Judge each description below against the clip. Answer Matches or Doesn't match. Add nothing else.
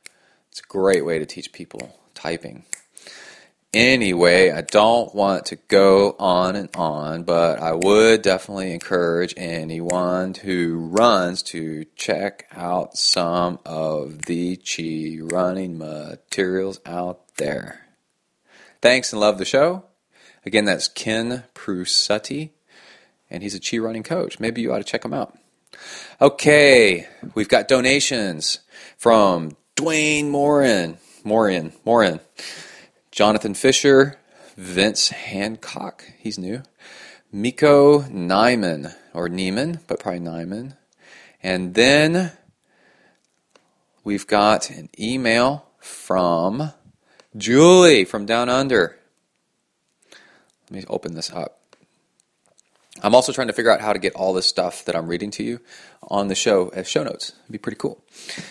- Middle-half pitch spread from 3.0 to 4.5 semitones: Doesn't match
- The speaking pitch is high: Doesn't match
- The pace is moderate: Doesn't match